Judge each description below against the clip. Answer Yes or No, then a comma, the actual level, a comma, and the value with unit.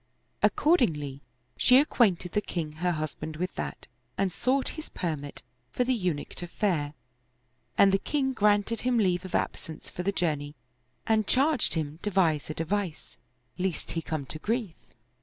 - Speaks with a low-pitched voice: No, medium, 180 Hz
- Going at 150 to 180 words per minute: Yes, average, 160 wpm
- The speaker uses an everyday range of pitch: No, wide, 6.0 semitones